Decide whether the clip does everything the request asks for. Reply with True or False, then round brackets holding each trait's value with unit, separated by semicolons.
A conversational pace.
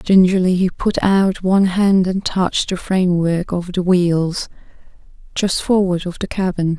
True (160 wpm)